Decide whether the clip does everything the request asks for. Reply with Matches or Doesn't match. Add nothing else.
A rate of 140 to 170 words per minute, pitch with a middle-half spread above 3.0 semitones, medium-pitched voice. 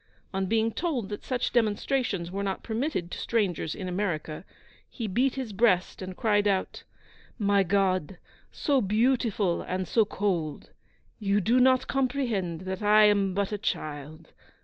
Doesn't match